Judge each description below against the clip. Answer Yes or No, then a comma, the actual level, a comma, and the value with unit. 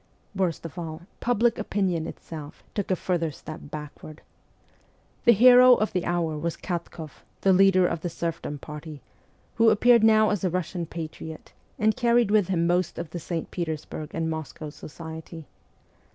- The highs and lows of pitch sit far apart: No, average, 4.1 semitones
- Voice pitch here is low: No, medium, 175 Hz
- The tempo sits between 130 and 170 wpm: Yes, average, 165 wpm